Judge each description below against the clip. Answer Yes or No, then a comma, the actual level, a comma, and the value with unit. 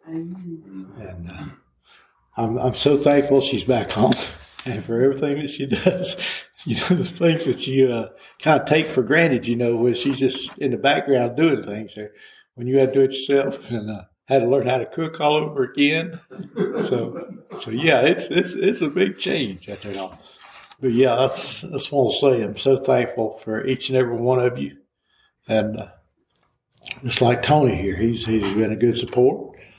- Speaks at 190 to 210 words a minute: Yes, average, 195 wpm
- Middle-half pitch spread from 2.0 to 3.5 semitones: No, average, 3.9 semitones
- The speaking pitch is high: No, low, 130 Hz